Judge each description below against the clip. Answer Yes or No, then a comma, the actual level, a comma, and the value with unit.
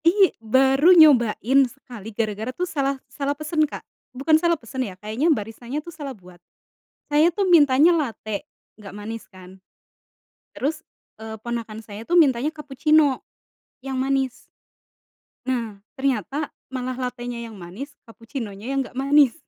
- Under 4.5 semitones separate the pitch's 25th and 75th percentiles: No, average, 4.8 semitones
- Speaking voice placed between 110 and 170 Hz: No, very high, 260 Hz